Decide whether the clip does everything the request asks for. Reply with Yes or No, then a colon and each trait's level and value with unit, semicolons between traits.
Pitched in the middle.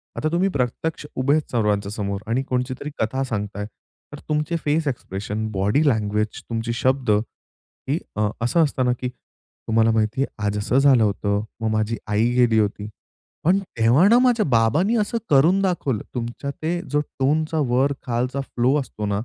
No: low, 125 Hz